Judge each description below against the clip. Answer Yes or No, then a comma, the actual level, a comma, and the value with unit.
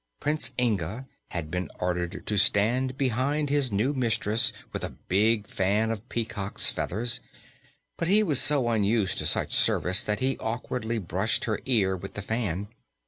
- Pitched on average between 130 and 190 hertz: No, low, 110 Hz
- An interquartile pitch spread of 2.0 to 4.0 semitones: No, average, 4.5 semitones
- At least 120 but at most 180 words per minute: Yes, average, 160 wpm